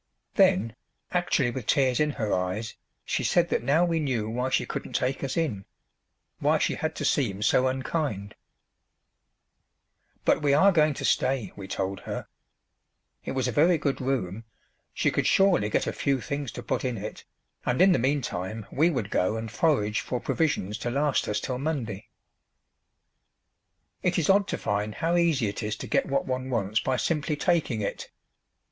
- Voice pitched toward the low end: Yes, low, 130 Hz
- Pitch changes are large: Yes, wide, 6.0 semitones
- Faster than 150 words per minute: Yes, average, 180 wpm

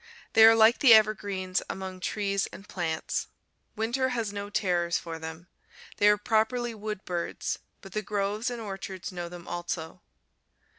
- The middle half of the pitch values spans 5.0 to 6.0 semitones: No, average, 3.4 semitones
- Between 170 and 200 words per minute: No, average, 155 wpm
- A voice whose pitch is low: No, high, 200 Hz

